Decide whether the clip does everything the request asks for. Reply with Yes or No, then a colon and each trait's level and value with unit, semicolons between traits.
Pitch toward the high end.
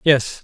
No: low, 135 Hz